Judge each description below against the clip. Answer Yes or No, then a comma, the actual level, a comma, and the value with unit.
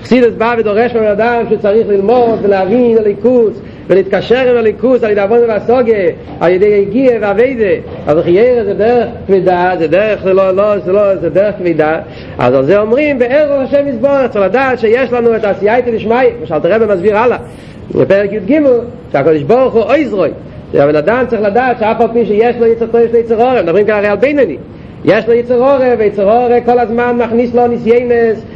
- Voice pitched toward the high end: Yes, high, 230 Hz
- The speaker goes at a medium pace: No, fast, 190 wpm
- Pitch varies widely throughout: No, average, 3.0 semitones